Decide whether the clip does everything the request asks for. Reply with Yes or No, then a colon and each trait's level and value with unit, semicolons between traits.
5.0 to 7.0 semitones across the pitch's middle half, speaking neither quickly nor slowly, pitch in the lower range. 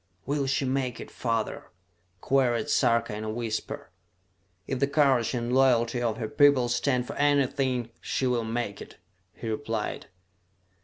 No: average, 2.8 semitones; average, 150 wpm; low, 125 Hz